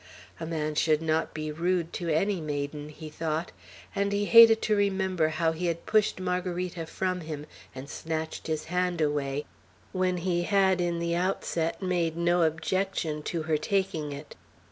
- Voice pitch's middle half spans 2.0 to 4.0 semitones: Yes, average, 2.9 semitones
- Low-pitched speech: No, medium, 170 Hz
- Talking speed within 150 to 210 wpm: Yes, average, 165 wpm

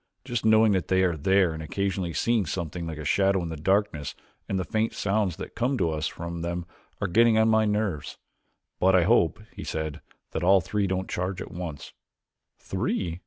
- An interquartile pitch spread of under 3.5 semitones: No, average, 3.8 semitones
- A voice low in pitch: Yes, very low, 95 Hz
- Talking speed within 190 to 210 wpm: Yes, average, 200 wpm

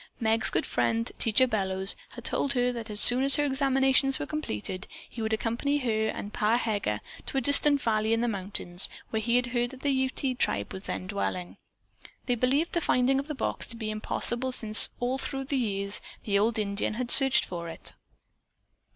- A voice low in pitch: No, high, 235 Hz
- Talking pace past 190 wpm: Yes, average, 200 wpm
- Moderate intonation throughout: Yes, average, 3.8 semitones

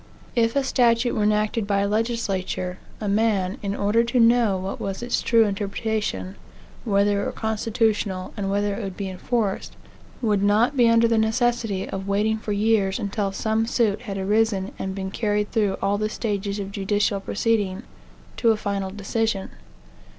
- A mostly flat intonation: Yes, narrow, 2.3 semitones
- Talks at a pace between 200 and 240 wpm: No, average, 170 wpm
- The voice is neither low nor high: No, high, 210 Hz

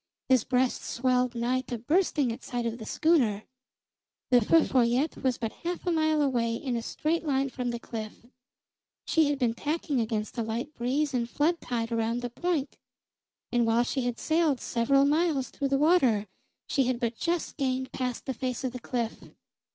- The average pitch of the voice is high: Yes, very high, 255 Hz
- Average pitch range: Yes, average, 3.6 semitones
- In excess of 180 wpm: Yes, average, 190 wpm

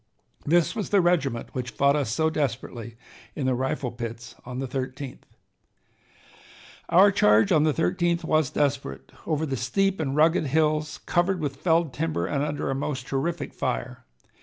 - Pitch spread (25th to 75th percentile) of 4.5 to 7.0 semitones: No, average, 3.8 semitones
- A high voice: No, medium, 140 Hz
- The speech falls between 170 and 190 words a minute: No, average, 160 wpm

